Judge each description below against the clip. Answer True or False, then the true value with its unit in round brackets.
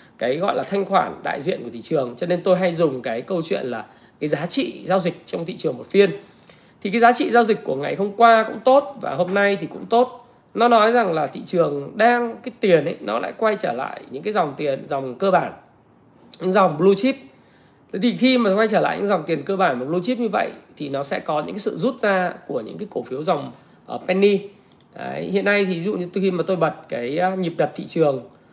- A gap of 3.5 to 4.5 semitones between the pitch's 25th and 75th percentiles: True (4.2 semitones)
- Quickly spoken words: True (255 wpm)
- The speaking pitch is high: True (200 Hz)